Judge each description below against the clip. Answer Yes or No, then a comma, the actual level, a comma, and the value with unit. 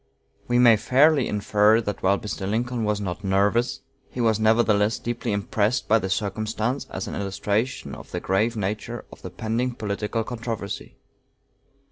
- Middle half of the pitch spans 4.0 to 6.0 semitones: No, narrow, 2.6 semitones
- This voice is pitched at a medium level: No, low, 110 Hz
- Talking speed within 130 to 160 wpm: Yes, average, 155 wpm